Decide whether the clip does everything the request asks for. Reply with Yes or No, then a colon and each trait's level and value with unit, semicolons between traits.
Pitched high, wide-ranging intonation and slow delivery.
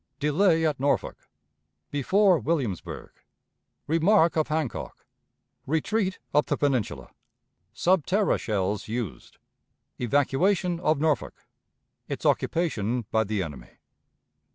No: medium, 150 Hz; wide, 6.9 semitones; slow, 100 wpm